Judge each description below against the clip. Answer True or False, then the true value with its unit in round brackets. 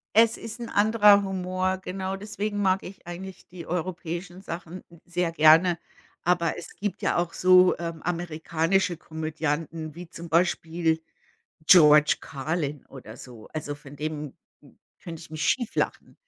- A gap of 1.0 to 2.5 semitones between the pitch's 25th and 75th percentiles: False (2.9 semitones)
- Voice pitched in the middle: True (170 Hz)